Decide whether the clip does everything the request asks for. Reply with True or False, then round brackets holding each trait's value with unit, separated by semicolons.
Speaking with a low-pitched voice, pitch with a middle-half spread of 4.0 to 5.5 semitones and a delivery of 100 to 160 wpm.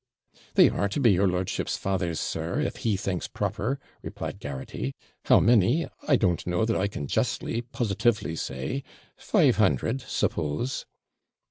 True (100 Hz; 5.1 semitones; 145 wpm)